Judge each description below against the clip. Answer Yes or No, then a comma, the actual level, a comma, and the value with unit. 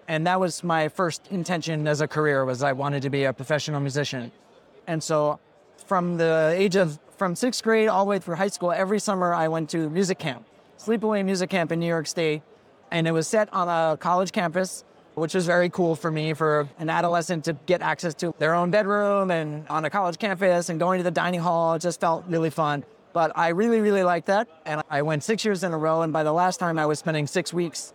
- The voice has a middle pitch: Yes, medium, 170 Hz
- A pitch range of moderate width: Yes, average, 3.0 semitones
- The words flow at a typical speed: No, fast, 235 wpm